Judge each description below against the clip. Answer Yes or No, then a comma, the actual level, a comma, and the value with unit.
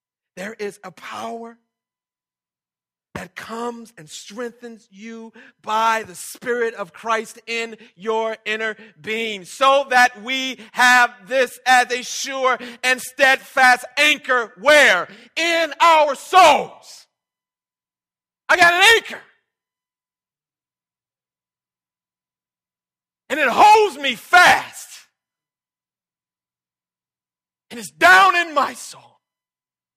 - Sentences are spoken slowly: Yes, slow, 95 wpm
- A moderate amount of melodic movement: Yes, average, 3.7 semitones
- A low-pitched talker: No, high, 240 Hz